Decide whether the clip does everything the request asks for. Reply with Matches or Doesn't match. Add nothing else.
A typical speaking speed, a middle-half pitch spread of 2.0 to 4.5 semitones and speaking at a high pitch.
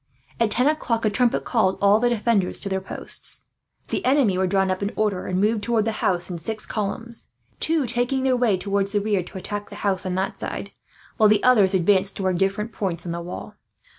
Doesn't match